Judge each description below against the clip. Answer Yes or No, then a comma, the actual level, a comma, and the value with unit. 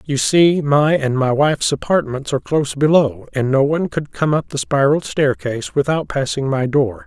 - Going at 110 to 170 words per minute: No, average, 195 wpm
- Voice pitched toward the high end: No, medium, 145 Hz